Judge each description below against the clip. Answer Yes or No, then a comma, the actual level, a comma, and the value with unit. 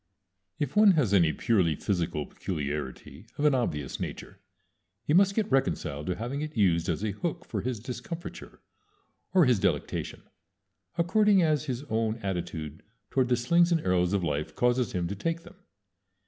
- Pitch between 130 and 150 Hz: No, low, 115 Hz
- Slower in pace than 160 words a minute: No, average, 165 wpm